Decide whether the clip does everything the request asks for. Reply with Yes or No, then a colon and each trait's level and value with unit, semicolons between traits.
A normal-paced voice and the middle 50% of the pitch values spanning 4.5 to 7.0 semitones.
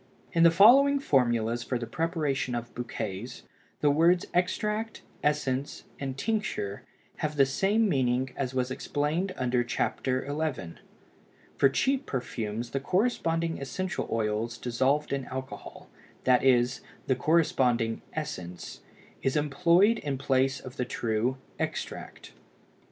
No: slow, 125 wpm; average, 5.1 semitones